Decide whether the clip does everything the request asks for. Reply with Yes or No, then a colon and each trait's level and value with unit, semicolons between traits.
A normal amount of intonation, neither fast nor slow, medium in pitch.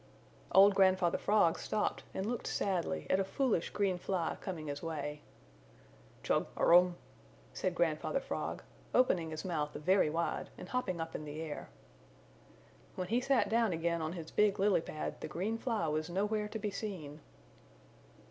Yes: average, 4.4 semitones; average, 160 wpm; medium, 180 Hz